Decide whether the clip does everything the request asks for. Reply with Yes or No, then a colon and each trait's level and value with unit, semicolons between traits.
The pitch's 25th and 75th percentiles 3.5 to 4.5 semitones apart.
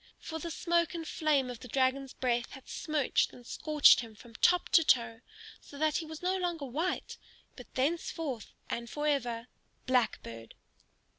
No: average, 4.9 semitones